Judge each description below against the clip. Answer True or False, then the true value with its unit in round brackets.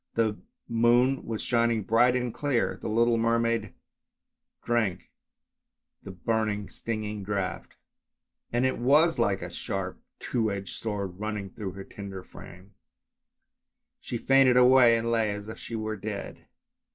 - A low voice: True (110 Hz)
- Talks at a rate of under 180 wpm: True (140 wpm)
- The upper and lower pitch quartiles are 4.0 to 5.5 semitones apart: False (2.8 semitones)